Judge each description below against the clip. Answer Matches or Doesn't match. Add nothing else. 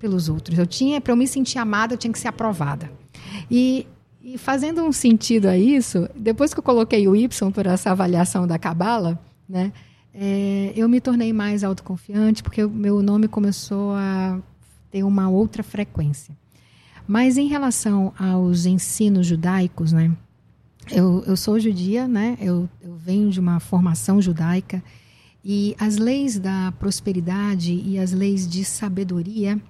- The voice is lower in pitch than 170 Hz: Doesn't match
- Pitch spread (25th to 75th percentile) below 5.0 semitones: Matches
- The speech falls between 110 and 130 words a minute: Doesn't match